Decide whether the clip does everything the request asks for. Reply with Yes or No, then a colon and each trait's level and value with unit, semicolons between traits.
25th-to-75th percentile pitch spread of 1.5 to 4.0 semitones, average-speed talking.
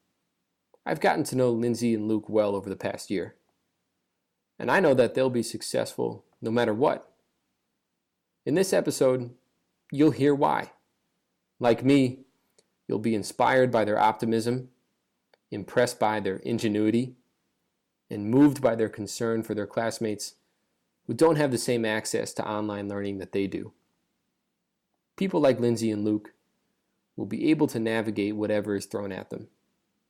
Yes: average, 3.0 semitones; average, 150 wpm